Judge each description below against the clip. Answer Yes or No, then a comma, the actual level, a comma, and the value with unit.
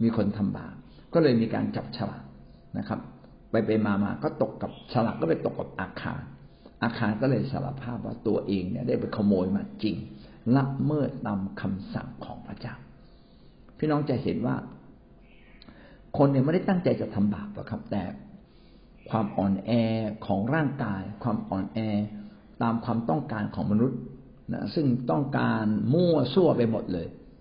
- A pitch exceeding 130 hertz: No, low, 115 Hz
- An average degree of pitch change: Yes, average, 4.1 semitones